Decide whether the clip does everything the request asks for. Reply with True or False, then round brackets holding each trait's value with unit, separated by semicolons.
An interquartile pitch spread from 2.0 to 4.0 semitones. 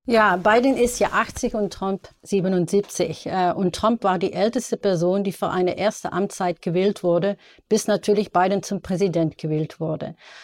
True (2.7 semitones)